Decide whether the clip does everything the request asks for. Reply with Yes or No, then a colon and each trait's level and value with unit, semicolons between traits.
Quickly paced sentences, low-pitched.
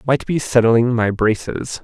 No: average, 165 wpm; low, 120 Hz